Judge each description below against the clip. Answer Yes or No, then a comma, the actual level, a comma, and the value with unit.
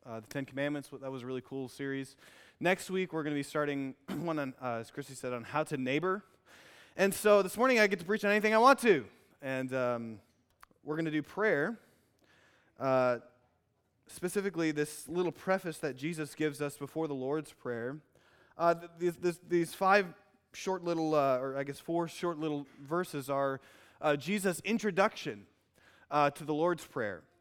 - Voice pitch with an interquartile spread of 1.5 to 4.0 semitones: No, average, 4.6 semitones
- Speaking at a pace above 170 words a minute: Yes, average, 185 wpm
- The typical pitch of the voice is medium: Yes, medium, 150 Hz